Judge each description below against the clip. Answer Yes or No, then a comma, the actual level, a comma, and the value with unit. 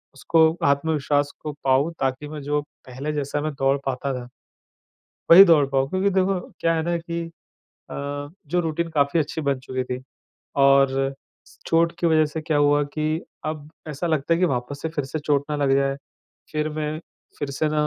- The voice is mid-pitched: Yes, medium, 150 Hz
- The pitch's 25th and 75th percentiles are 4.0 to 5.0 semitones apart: No, average, 2.7 semitones